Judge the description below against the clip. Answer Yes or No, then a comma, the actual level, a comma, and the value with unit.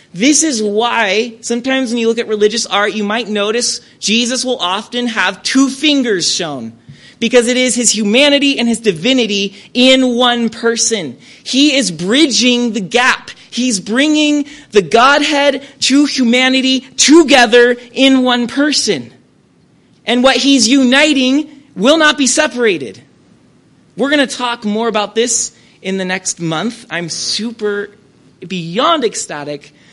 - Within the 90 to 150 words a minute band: Yes, average, 140 wpm